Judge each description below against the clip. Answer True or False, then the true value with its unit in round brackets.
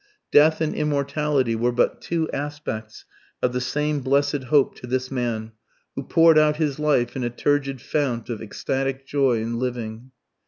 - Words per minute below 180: True (165 wpm)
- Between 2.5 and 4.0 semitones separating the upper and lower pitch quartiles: True (3.4 semitones)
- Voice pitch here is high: False (135 Hz)